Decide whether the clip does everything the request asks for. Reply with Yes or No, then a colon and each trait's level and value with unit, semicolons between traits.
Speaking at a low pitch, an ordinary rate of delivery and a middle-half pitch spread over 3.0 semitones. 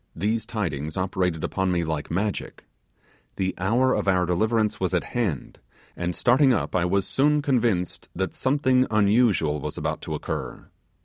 Yes: low, 100 Hz; average, 160 wpm; average, 5.2 semitones